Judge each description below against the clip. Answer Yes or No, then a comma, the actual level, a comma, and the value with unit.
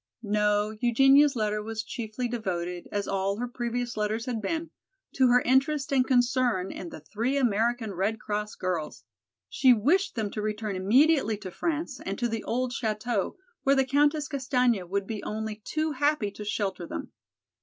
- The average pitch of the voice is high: Yes, high, 225 Hz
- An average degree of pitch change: Yes, average, 3.9 semitones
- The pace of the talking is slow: No, average, 170 wpm